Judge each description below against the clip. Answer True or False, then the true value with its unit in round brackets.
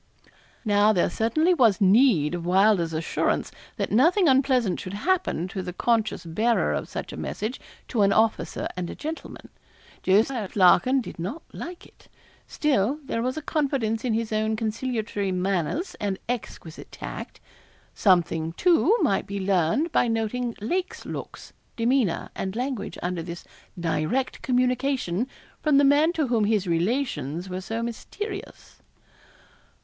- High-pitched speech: True (220 Hz)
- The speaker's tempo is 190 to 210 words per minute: False (145 wpm)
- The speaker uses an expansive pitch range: True (6.0 semitones)